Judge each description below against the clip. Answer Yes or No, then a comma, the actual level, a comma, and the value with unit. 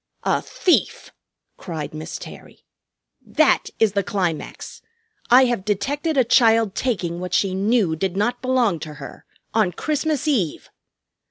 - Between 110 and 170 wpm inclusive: Yes, average, 140 wpm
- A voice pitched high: Yes, high, 210 Hz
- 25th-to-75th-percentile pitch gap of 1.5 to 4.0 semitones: No, wide, 5.6 semitones